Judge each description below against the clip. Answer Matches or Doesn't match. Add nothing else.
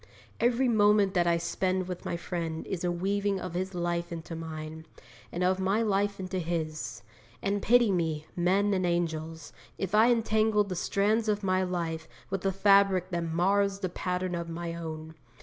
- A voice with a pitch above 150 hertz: Matches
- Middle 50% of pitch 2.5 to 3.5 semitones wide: Matches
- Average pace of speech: Matches